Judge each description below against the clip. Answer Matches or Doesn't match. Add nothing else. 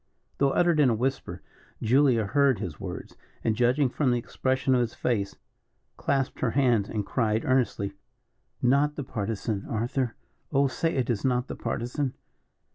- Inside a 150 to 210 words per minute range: Matches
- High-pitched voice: Doesn't match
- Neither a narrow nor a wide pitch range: Matches